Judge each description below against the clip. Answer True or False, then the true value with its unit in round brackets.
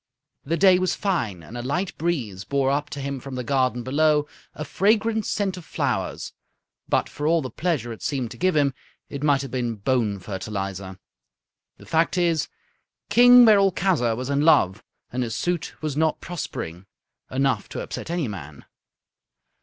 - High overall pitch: False (140 Hz)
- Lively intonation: True (6.4 semitones)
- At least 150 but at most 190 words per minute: True (170 wpm)